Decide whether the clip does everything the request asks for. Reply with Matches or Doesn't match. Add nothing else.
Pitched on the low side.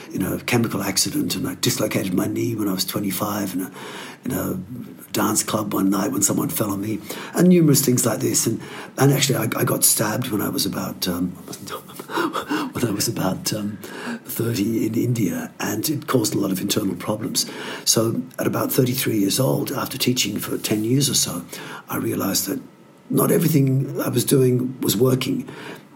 Matches